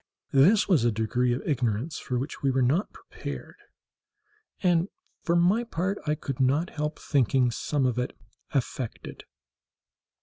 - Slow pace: No, average, 145 wpm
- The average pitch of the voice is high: No, medium, 140 Hz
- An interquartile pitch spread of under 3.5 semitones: No, average, 5.2 semitones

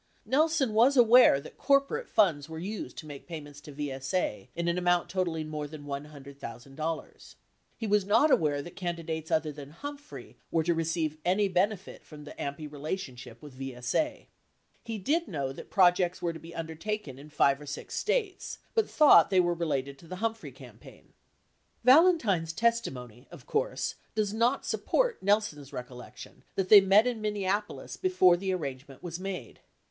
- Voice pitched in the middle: Yes, medium, 170 Hz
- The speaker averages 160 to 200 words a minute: Yes, average, 170 wpm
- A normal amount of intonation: No, wide, 6.5 semitones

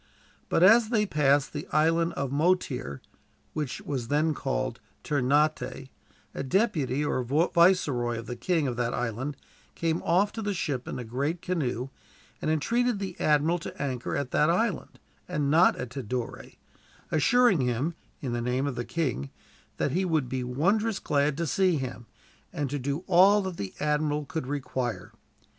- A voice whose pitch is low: No, medium, 145 Hz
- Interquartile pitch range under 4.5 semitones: No, average, 5.0 semitones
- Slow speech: No, average, 165 wpm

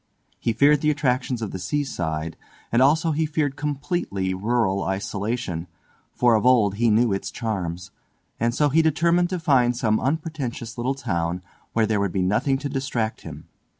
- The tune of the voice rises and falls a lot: Yes, wide, 6.4 semitones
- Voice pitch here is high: No, low, 120 Hz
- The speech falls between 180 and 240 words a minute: No, average, 170 wpm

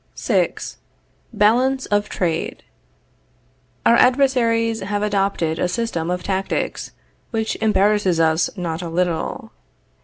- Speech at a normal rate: No, slow, 110 wpm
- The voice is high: Yes, high, 205 Hz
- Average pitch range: Yes, average, 4.4 semitones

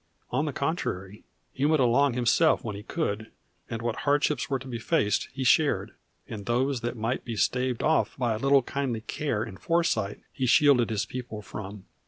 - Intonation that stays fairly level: No, average, 4.2 semitones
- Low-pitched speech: Yes, low, 125 Hz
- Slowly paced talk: No, average, 190 wpm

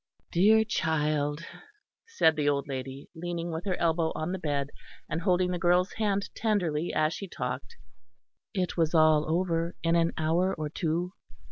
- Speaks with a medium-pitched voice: Yes, medium, 165 Hz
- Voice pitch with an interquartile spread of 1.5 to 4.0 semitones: Yes, average, 2.8 semitones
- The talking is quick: No, average, 160 wpm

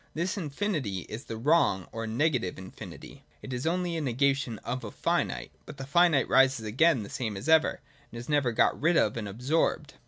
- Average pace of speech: Yes, average, 195 wpm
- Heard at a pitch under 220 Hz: Yes, low, 135 Hz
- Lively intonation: Yes, wide, 5.9 semitones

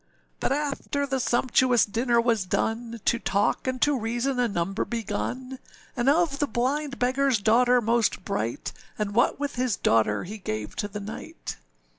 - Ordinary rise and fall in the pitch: Yes, average, 4.0 semitones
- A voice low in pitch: No, high, 240 Hz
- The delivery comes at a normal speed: Yes, average, 165 wpm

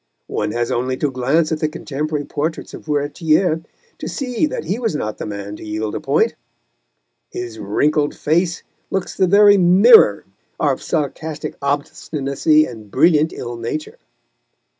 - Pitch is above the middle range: No, medium, 150 Hz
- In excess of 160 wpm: No, average, 150 wpm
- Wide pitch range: No, average, 4.5 semitones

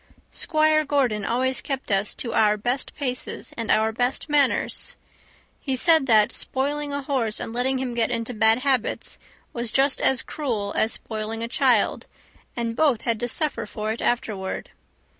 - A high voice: Yes, high, 245 Hz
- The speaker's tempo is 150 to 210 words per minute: Yes, average, 165 wpm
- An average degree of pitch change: Yes, average, 3.5 semitones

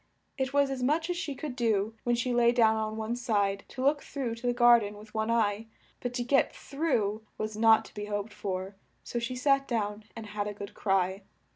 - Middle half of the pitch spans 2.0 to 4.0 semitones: Yes, average, 3.3 semitones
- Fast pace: Yes, fast, 230 wpm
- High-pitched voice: Yes, high, 230 Hz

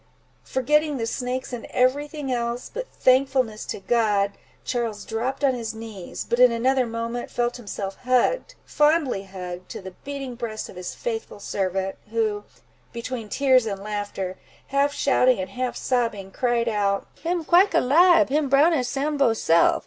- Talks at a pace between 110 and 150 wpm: No, average, 160 wpm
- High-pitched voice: Yes, high, 240 Hz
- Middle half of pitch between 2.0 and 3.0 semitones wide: No, average, 4.2 semitones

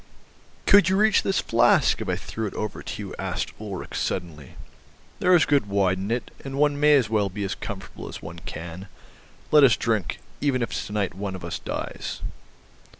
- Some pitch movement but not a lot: No, wide, 6.9 semitones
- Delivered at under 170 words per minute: No, average, 200 wpm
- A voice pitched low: Yes, low, 105 Hz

